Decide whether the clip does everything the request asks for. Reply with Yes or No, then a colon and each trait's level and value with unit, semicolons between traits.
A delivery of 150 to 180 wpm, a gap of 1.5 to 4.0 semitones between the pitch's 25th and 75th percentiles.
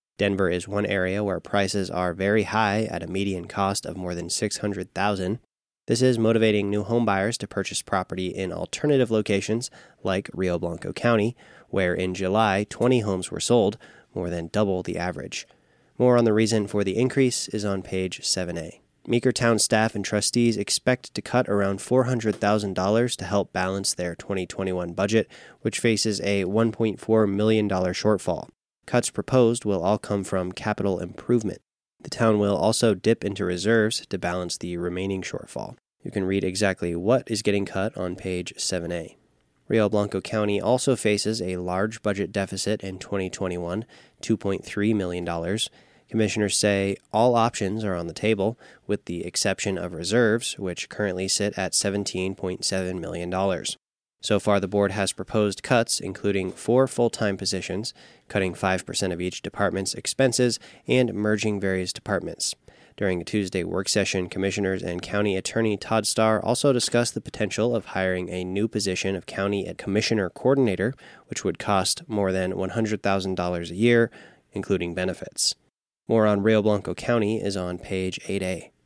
Yes: average, 165 wpm; average, 2.8 semitones